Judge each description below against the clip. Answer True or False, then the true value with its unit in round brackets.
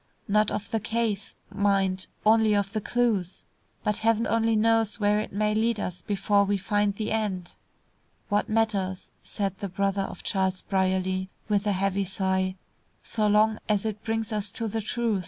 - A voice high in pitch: True (205 Hz)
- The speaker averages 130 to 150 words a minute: False (175 wpm)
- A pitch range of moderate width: False (2.1 semitones)